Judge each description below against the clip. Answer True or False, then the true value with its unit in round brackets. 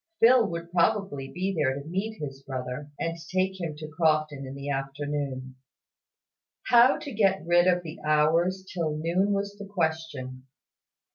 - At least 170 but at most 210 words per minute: False (155 wpm)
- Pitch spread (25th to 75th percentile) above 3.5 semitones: True (4.7 semitones)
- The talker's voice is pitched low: False (160 Hz)